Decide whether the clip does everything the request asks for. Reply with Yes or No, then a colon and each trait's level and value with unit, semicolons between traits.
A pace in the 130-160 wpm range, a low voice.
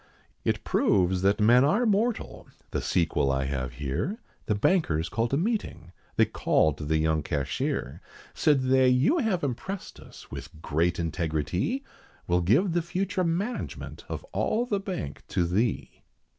Yes: average, 150 wpm; low, 115 Hz